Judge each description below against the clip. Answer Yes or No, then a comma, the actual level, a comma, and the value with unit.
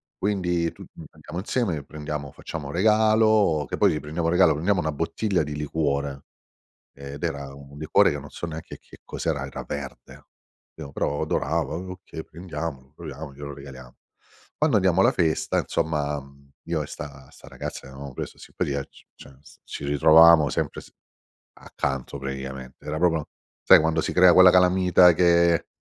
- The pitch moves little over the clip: No, average, 3.7 semitones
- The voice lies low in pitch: Yes, very low, 80 Hz